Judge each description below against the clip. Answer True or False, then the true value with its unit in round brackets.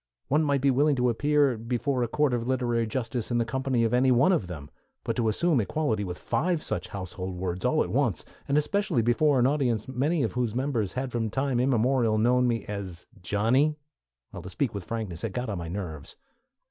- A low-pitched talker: True (120 Hz)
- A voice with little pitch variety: False (4.2 semitones)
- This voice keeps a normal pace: False (210 wpm)